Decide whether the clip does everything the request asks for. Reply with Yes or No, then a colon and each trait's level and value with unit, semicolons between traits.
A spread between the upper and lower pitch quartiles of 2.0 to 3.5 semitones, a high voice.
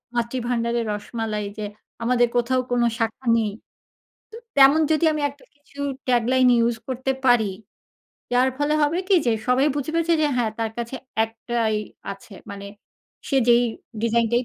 Yes: average, 2.8 semitones; high, 240 Hz